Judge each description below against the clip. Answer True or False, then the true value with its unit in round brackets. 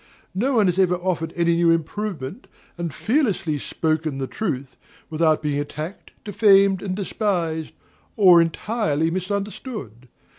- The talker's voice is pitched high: False (175 Hz)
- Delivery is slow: True (125 wpm)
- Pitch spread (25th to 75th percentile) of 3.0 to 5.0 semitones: True (4.3 semitones)